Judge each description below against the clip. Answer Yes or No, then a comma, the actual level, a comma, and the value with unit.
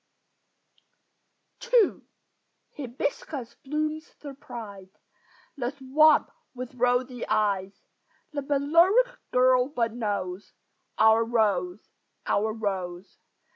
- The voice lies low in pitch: No, high, 245 Hz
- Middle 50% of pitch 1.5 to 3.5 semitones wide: No, average, 5.2 semitones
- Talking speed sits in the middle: No, slow, 80 wpm